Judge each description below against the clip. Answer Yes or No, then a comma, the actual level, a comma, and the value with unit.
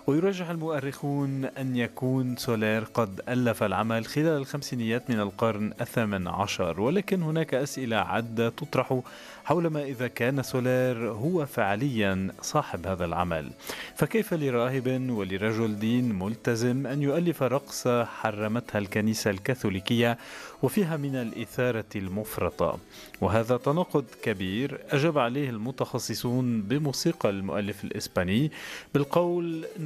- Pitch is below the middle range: Yes, low, 125 Hz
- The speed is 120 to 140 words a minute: No, average, 110 wpm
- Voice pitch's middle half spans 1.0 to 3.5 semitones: No, average, 4.3 semitones